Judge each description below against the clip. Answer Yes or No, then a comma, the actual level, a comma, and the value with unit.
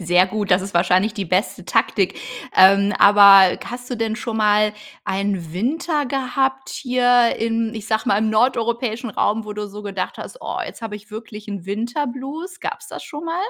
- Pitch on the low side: No, high, 220 Hz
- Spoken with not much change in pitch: No, average, 3.7 semitones